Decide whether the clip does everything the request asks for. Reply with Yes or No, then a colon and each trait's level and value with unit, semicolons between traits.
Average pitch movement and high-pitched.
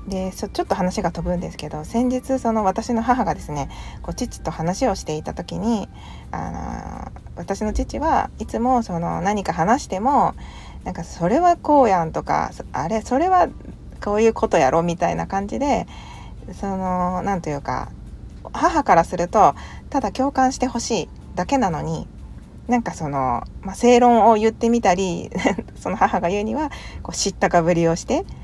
No: wide, 5.8 semitones; high, 195 Hz